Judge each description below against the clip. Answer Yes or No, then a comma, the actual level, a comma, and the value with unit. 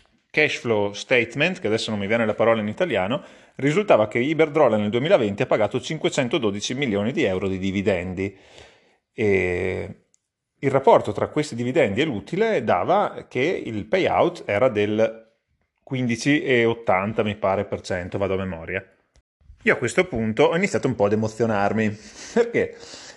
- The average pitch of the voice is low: Yes, low, 110 Hz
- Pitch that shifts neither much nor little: Yes, average, 4.5 semitones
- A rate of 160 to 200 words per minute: No, average, 150 wpm